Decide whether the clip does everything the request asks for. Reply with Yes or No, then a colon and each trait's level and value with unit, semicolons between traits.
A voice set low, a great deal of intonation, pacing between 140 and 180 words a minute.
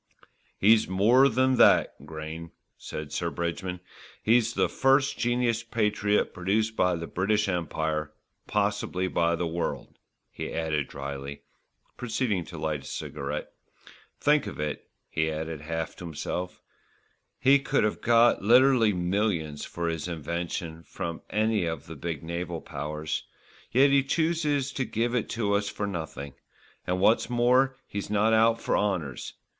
Yes: very low, 95 Hz; wide, 6.1 semitones; average, 145 wpm